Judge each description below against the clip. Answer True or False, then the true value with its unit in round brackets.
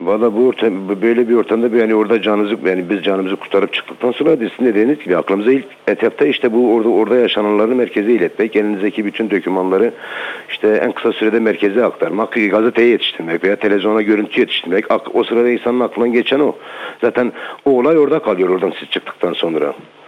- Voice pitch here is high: False (110 Hz)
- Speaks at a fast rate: True (175 wpm)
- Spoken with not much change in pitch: True (2.3 semitones)